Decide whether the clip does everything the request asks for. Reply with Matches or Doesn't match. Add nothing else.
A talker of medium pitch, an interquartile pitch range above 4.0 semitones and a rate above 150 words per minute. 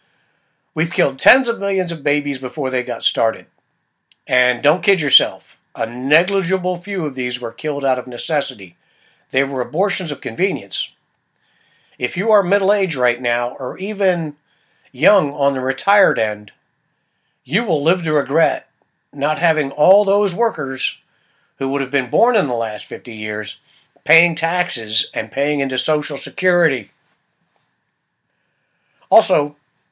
Doesn't match